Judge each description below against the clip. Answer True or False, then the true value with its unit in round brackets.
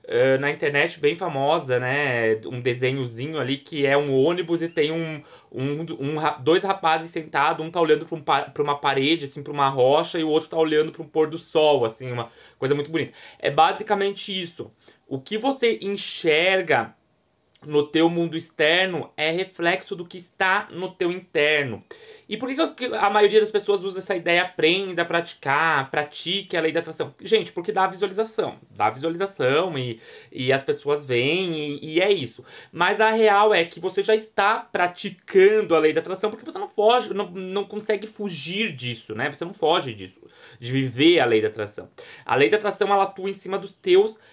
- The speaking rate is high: True (190 wpm)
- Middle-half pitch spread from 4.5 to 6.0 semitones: True (5.2 semitones)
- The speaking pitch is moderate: True (170 Hz)